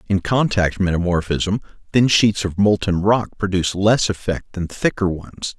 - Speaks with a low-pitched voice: Yes, very low, 95 Hz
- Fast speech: No, average, 150 wpm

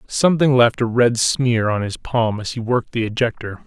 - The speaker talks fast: Yes, fast, 215 wpm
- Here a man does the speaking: Yes, male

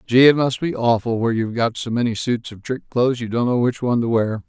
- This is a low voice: Yes, low, 120 Hz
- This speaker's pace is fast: Yes, fast, 280 wpm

